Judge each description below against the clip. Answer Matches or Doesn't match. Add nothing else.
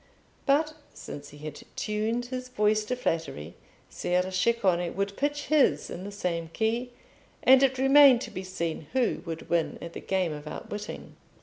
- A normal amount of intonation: Doesn't match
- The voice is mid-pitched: Doesn't match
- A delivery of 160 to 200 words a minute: Matches